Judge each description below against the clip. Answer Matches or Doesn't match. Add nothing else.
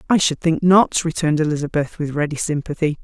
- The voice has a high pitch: Doesn't match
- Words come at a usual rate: Matches